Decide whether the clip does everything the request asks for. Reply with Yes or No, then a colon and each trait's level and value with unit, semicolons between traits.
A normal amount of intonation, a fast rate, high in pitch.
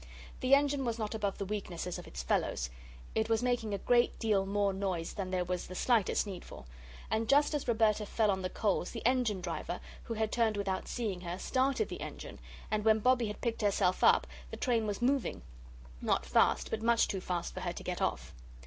Yes: average, 3.7 semitones; fast, 215 wpm; high, 215 Hz